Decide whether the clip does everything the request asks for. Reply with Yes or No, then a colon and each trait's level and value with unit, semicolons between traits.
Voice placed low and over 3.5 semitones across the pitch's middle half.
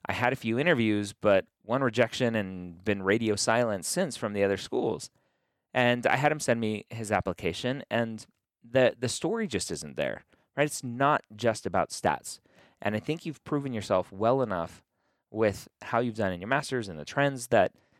Yes: low, 115 Hz; average, 4.0 semitones